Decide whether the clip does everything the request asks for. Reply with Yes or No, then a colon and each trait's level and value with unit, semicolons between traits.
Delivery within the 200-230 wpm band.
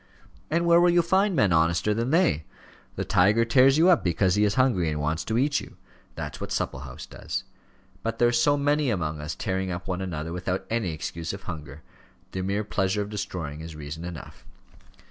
Yes: fast, 205 wpm